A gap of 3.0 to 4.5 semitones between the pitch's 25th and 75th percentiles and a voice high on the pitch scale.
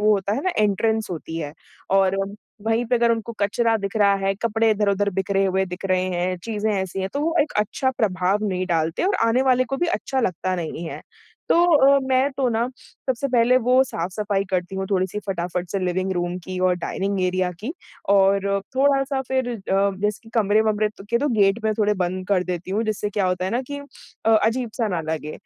Yes: average, 3.8 semitones; high, 205 Hz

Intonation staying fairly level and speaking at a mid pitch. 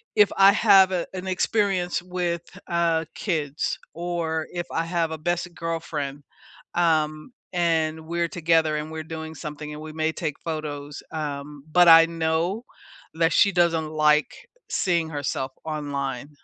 Yes: narrow, 2.1 semitones; medium, 160 Hz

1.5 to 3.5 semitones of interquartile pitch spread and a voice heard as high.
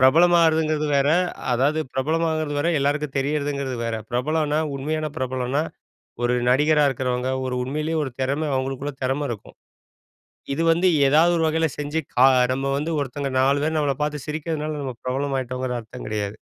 No: average, 2.9 semitones; medium, 145 Hz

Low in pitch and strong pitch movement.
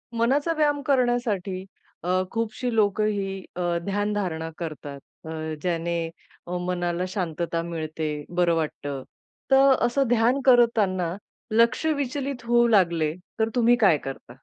No: high, 200 Hz; wide, 5.9 semitones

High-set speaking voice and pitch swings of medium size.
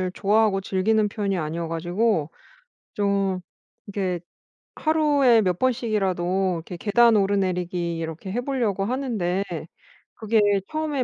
Yes: high, 200 Hz; average, 4.2 semitones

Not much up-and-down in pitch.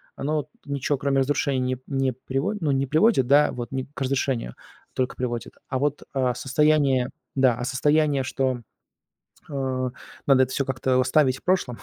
Yes: narrow, 1.9 semitones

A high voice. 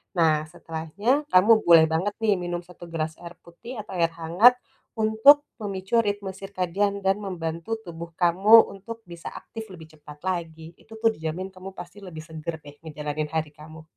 No: medium, 175 Hz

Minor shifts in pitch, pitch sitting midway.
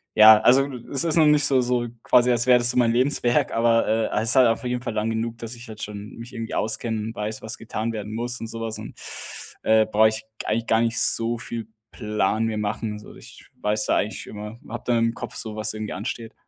No: narrow, 1.9 semitones; low, 115 Hz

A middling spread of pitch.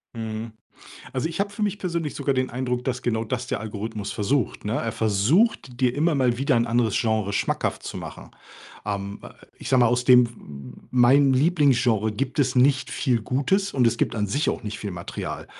Yes: average, 3.9 semitones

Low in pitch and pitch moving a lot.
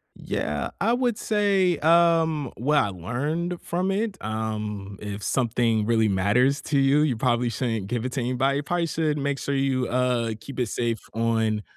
Yes: low, 130 Hz; wide, 5.7 semitones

